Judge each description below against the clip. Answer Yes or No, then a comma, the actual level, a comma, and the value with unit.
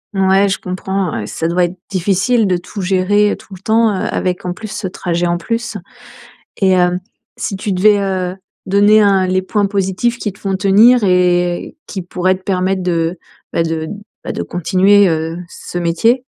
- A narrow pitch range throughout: Yes, narrow, 2.2 semitones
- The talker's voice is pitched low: No, high, 190 Hz